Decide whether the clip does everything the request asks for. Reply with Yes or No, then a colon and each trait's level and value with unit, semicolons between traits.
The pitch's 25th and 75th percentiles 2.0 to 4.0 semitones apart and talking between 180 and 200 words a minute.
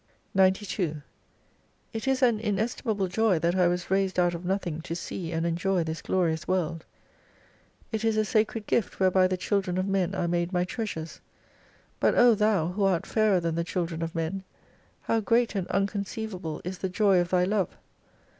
Yes: average, 3.2 semitones; average, 185 wpm